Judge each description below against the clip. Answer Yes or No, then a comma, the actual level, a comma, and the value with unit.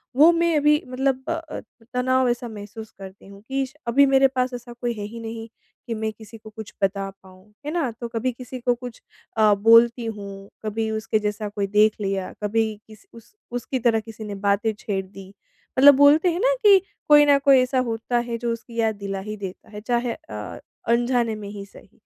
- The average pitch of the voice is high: Yes, high, 230 Hz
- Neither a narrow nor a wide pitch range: Yes, average, 3.6 semitones